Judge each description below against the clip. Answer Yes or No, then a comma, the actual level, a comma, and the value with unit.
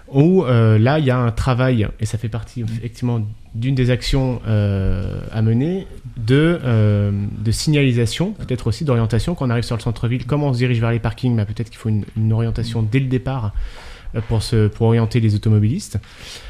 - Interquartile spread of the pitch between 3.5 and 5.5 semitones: No, narrow, 2.5 semitones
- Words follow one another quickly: No, average, 200 wpm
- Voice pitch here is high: No, low, 115 Hz